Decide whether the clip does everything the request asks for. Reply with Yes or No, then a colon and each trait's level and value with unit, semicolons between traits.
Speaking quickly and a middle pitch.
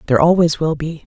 Yes: fast, 210 wpm; medium, 160 Hz